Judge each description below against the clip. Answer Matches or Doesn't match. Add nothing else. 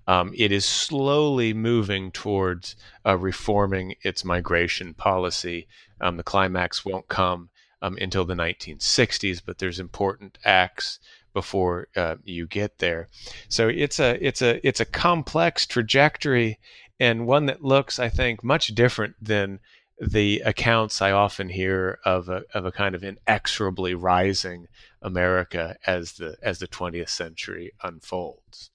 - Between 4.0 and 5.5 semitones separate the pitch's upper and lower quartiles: Doesn't match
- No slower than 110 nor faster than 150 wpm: Matches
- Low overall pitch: Matches